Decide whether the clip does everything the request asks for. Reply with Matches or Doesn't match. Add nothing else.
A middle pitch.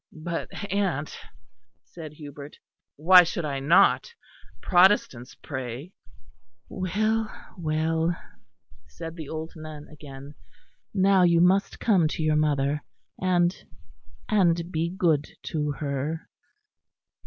Matches